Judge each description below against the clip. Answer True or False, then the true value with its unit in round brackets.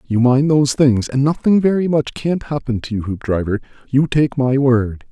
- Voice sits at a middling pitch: False (130 Hz)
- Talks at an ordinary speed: True (190 wpm)